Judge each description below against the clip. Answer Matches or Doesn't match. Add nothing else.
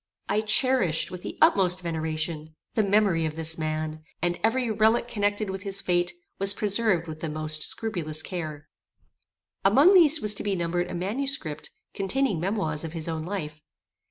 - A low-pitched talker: Doesn't match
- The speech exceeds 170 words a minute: Doesn't match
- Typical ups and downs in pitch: Matches